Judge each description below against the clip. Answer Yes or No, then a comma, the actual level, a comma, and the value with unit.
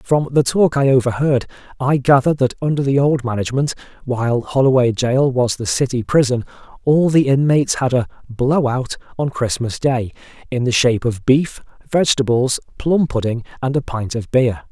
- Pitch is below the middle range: Yes, low, 130 Hz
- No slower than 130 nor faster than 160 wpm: No, average, 170 wpm